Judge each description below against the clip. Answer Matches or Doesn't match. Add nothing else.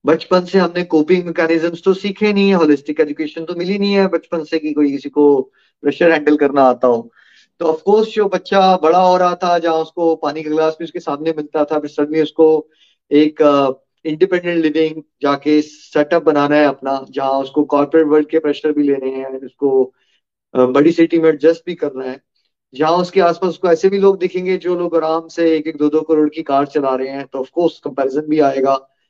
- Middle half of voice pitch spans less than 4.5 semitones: Matches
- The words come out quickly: Matches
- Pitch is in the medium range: Matches